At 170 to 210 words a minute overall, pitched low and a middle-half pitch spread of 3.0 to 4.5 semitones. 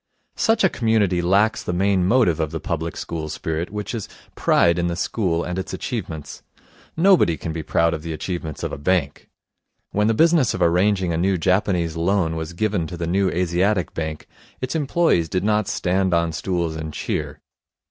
Yes: average, 190 wpm; very low, 90 Hz; average, 3.8 semitones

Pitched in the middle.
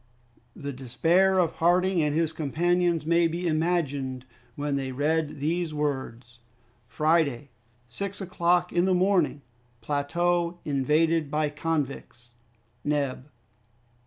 Yes: medium, 155 Hz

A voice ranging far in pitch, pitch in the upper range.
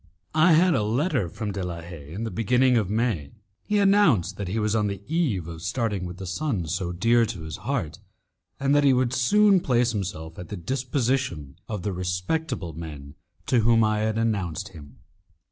No: wide, 6.5 semitones; low, 105 Hz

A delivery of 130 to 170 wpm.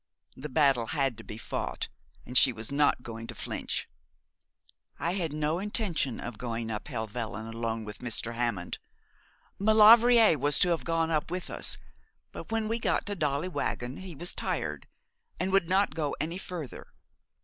Yes: average, 165 wpm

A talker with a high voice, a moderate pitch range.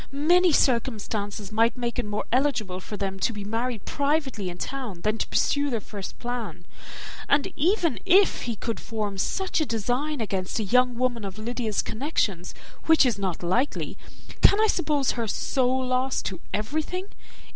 Yes: high, 235 Hz; average, 5.0 semitones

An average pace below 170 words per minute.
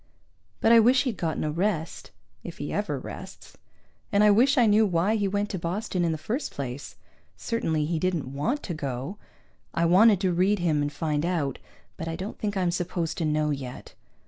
No: average, 200 wpm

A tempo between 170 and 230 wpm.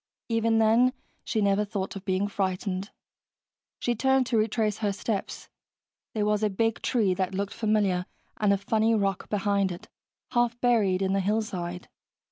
No: average, 160 wpm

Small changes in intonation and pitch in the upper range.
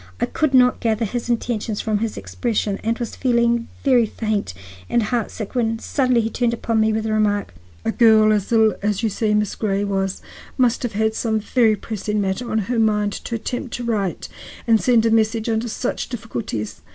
Yes: narrow, 1.9 semitones; high, 220 Hz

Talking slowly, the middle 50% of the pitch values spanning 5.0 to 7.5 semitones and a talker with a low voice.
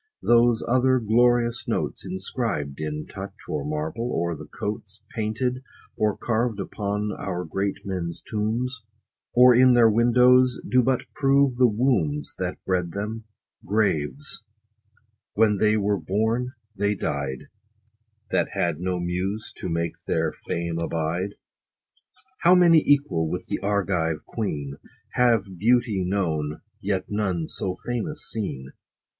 Yes: slow, 130 wpm; wide, 5.6 semitones; low, 105 Hz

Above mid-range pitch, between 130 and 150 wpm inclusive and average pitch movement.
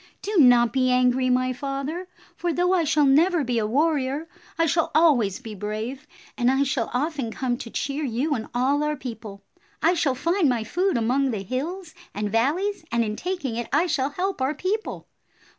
No: very high, 270 Hz; average, 190 wpm; average, 4.9 semitones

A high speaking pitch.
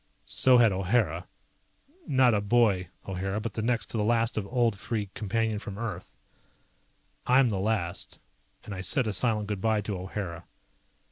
No: low, 105 Hz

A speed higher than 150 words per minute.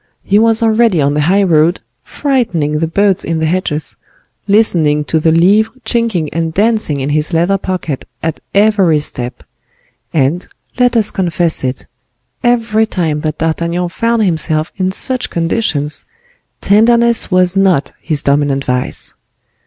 No: average, 145 wpm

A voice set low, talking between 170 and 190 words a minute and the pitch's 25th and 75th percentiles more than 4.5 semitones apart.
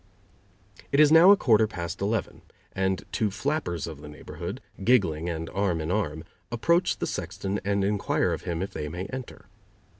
Yes: very low, 95 Hz; average, 175 wpm; average, 5.2 semitones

